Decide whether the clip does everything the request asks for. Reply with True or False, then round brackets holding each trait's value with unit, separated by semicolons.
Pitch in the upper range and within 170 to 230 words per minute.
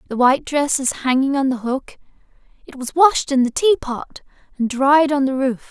True (270 Hz; 200 wpm)